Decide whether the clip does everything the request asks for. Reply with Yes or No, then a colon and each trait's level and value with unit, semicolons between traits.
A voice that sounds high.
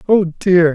No: medium, 175 Hz